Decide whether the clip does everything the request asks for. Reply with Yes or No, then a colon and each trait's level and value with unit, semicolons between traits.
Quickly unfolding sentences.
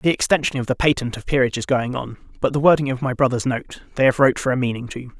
Yes: fast, 275 wpm